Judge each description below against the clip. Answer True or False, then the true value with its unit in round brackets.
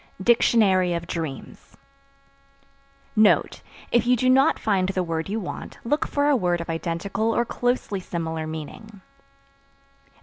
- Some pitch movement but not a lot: False (5.8 semitones)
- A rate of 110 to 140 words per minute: True (135 wpm)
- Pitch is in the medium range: False (195 Hz)